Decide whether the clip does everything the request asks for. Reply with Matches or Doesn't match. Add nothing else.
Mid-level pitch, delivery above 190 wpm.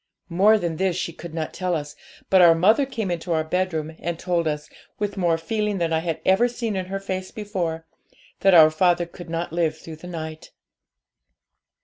Matches